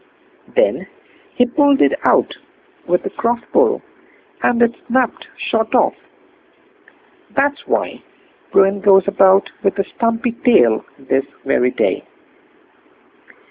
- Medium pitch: No, high, 225 Hz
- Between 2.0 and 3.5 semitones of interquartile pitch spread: No, average, 4.4 semitones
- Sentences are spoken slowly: Yes, slow, 115 wpm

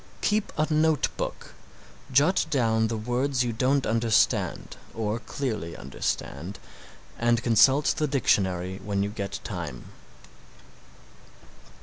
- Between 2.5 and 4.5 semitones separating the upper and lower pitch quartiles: No, average, 5.1 semitones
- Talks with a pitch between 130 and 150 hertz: No, low, 115 Hz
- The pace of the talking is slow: Yes, slow, 110 wpm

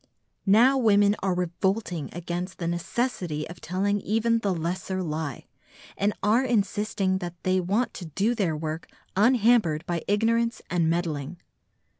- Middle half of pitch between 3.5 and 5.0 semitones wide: Yes, average, 3.9 semitones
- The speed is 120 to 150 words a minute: Yes, average, 140 wpm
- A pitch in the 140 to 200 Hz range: Yes, high, 190 Hz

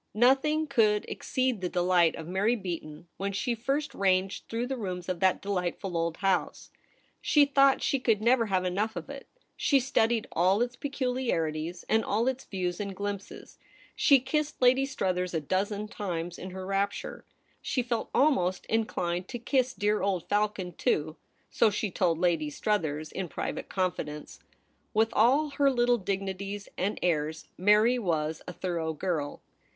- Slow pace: No, average, 160 wpm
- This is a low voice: No, high, 200 Hz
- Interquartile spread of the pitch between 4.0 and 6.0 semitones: Yes, average, 5.2 semitones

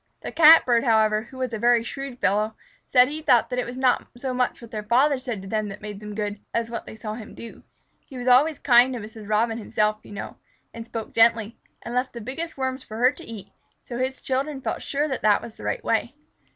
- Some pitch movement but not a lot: Yes, average, 3.1 semitones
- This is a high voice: Yes, high, 235 Hz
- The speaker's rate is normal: No, fast, 240 wpm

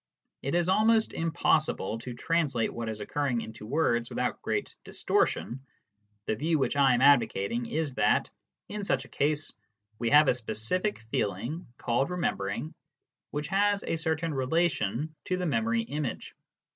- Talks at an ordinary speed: Yes, average, 150 wpm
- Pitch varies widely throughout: Yes, wide, 5.9 semitones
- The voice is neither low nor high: Yes, medium, 145 Hz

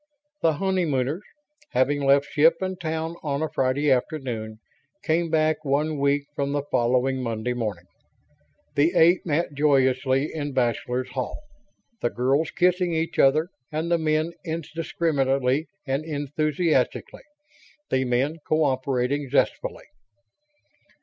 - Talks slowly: Yes, slow, 120 wpm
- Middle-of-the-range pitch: Yes, medium, 145 Hz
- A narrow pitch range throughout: No, average, 3.4 semitones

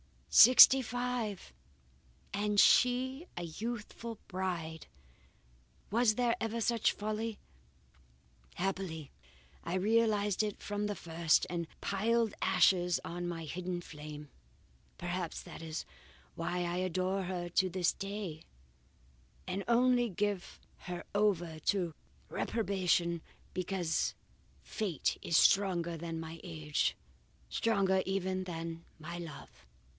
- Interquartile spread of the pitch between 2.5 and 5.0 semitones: Yes, average, 3.7 semitones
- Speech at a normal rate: No, slow, 110 wpm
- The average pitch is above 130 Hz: Yes, medium, 185 Hz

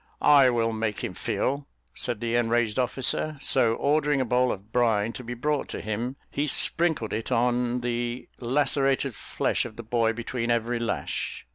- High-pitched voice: No, low, 120 Hz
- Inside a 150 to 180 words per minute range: Yes, average, 170 wpm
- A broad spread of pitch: No, narrow, 2.4 semitones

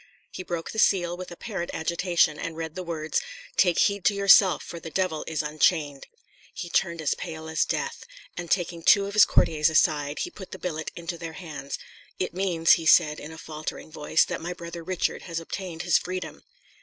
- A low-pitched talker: No, medium, 170 Hz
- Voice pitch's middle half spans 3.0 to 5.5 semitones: No, narrow, 2.4 semitones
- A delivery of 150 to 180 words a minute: No, average, 200 wpm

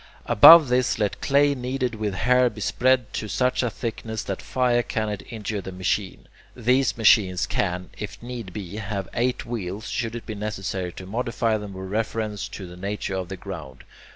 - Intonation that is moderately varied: Yes, average, 4.0 semitones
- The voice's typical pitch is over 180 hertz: No, low, 110 Hz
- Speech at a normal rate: Yes, average, 180 wpm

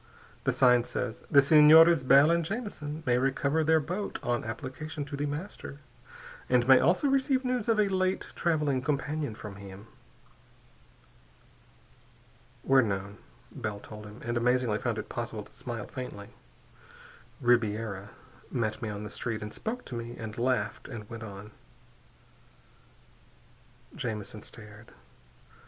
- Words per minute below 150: Yes, average, 140 wpm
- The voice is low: Yes, low, 125 Hz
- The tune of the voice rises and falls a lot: Yes, wide, 6.1 semitones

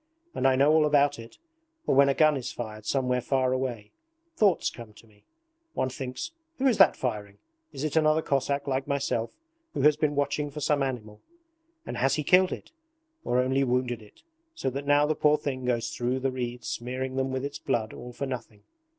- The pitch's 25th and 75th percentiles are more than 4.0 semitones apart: No, average, 2.8 semitones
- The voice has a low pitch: Yes, low, 130 Hz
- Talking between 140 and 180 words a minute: No, fast, 205 wpm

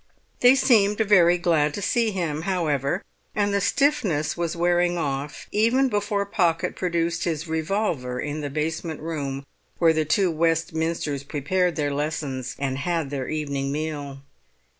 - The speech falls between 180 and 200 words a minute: No, average, 145 wpm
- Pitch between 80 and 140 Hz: No, medium, 165 Hz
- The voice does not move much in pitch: No, average, 4.1 semitones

